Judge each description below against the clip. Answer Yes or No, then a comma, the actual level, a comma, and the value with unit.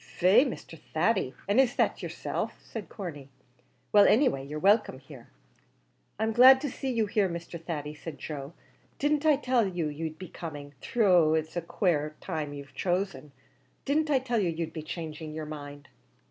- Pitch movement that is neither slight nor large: No, wide, 6.5 semitones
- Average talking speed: Yes, average, 175 wpm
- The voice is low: No, medium, 170 Hz